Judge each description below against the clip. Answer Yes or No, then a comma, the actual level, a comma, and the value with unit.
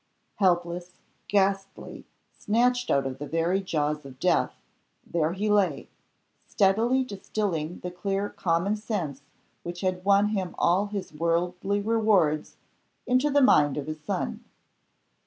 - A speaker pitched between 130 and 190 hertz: Yes, medium, 185 Hz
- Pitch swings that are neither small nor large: Yes, average, 3.8 semitones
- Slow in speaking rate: Yes, slow, 130 wpm